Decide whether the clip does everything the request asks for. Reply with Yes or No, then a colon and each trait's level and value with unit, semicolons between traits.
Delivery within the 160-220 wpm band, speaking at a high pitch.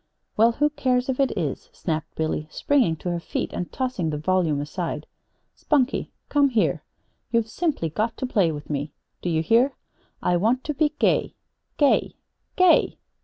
Yes: average, 170 wpm; high, 215 Hz